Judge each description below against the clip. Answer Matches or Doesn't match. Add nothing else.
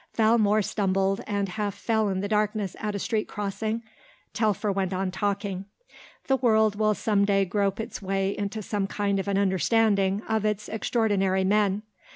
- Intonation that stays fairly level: Matches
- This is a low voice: Doesn't match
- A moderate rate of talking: Matches